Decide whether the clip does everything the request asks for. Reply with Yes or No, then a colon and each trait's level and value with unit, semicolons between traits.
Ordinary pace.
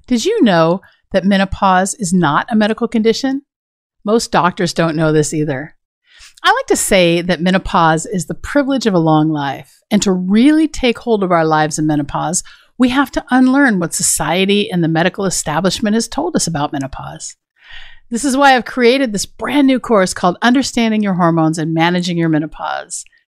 Yes: average, 180 wpm